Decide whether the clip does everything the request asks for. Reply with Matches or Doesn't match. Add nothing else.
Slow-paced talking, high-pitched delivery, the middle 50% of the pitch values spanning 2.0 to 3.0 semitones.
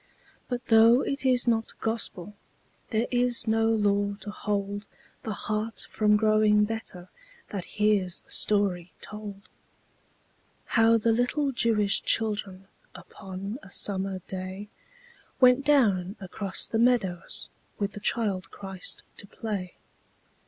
Matches